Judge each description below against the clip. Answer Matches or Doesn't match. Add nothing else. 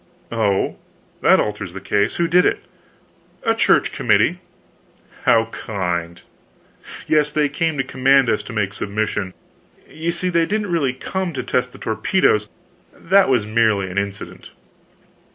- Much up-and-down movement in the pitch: Matches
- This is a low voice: Matches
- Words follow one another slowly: Doesn't match